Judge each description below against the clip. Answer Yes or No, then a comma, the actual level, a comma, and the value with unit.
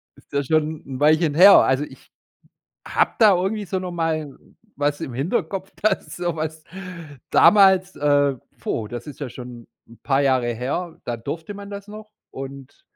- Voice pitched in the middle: Yes, medium, 155 Hz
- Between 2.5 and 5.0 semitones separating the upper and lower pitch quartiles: No, wide, 5.6 semitones